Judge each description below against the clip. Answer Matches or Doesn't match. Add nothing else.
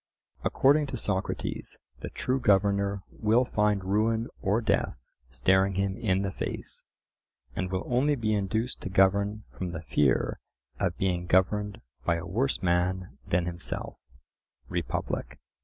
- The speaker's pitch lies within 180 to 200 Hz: Doesn't match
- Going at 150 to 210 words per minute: Doesn't match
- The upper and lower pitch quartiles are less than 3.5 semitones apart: Matches